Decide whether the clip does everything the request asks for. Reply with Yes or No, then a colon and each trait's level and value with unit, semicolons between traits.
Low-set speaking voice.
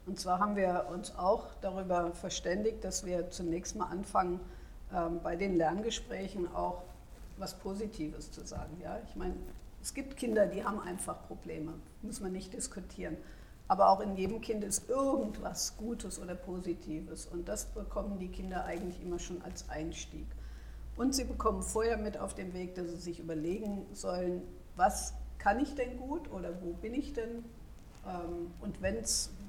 No: medium, 185 Hz